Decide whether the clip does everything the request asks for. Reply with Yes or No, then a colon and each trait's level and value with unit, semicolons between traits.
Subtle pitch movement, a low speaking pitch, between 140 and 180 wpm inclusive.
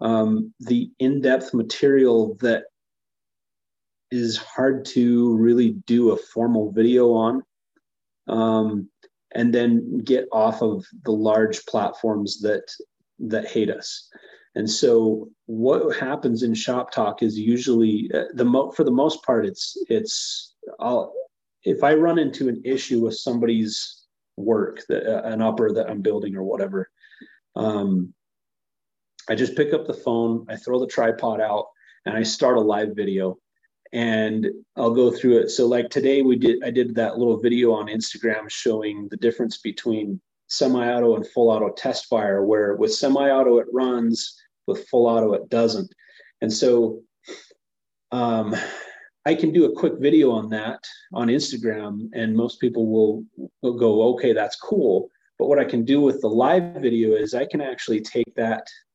Yes: narrow, 2.3 semitones; low, 115 Hz; average, 160 wpm